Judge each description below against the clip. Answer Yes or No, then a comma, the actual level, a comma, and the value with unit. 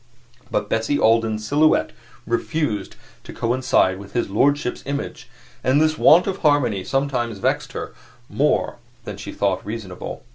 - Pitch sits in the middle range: No, low, 120 Hz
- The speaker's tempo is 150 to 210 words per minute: No, average, 140 wpm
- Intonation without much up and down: No, wide, 5.4 semitones